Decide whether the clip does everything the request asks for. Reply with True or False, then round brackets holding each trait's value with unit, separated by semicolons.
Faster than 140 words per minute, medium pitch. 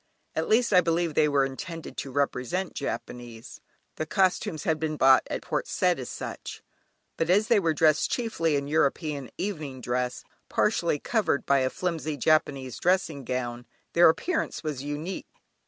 True (160 wpm; 155 Hz)